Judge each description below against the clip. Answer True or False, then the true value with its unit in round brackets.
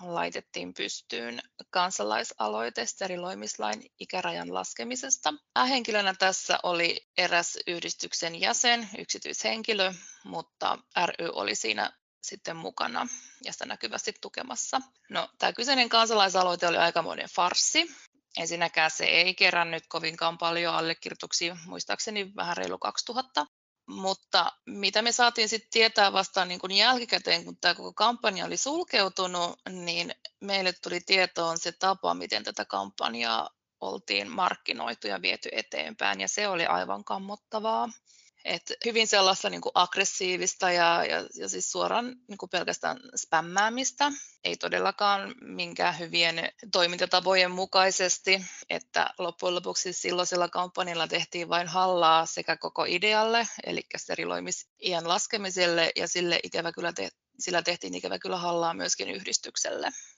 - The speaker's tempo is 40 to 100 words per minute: False (120 wpm)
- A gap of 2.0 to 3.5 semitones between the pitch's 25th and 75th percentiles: False (3.9 semitones)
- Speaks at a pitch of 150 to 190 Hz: True (185 Hz)